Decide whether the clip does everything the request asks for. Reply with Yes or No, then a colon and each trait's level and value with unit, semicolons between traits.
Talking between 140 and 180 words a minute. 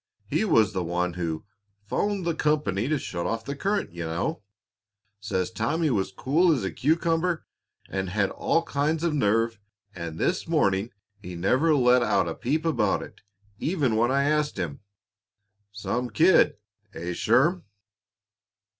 Yes: average, 155 wpm